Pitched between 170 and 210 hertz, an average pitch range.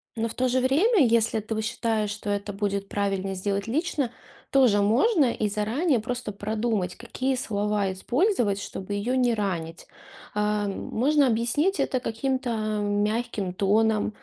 No: high, 220 Hz; average, 3.6 semitones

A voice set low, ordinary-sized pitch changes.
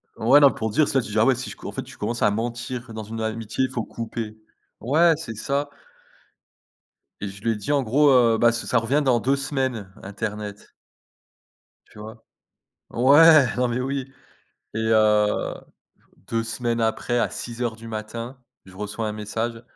Yes: low, 115 Hz; average, 3.0 semitones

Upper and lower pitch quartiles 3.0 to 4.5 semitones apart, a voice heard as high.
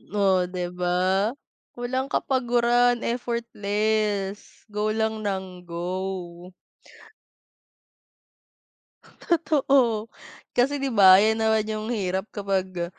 Yes: average, 3.9 semitones; high, 210 Hz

